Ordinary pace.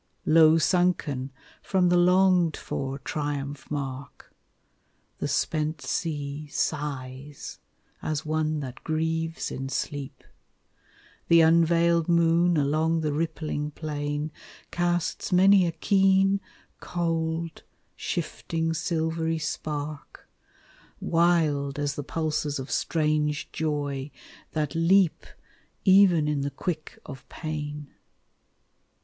No: slow, 100 wpm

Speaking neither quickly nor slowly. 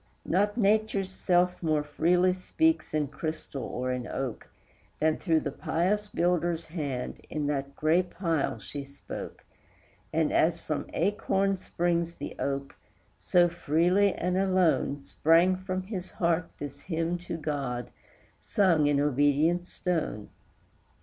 No: slow, 130 wpm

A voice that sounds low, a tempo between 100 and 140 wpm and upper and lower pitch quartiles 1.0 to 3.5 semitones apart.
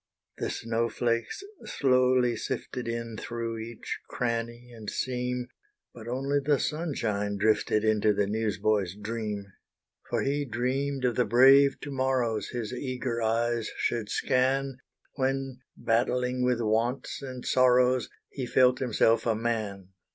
Yes: low, 120 Hz; slow, 135 wpm; narrow, 2.4 semitones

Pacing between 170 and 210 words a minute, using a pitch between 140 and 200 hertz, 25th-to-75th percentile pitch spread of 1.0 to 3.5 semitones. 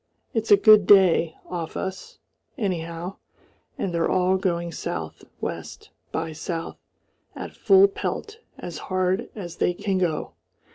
No: slow, 135 wpm; medium, 185 Hz; average, 3.0 semitones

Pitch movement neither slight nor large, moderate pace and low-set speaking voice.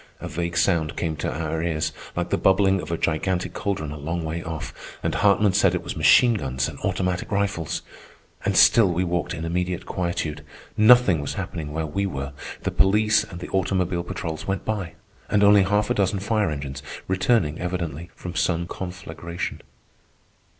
Yes: average, 3.3 semitones; average, 180 wpm; very low, 90 Hz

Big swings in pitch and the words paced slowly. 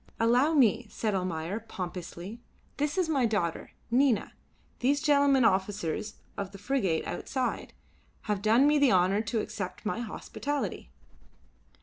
Yes: wide, 5.9 semitones; slow, 130 wpm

